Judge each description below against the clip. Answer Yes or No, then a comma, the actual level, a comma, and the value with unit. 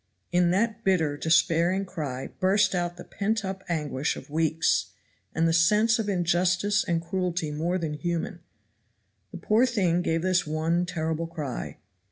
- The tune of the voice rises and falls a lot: No, average, 2.8 semitones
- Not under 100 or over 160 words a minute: Yes, average, 155 wpm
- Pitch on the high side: No, medium, 175 Hz